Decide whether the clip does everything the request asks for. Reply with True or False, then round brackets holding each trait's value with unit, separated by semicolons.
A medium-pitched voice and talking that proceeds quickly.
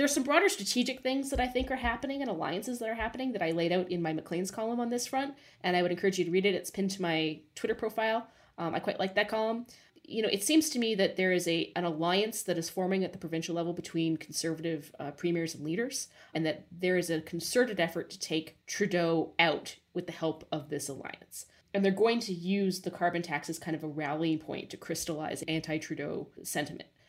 True (180 Hz; 235 wpm)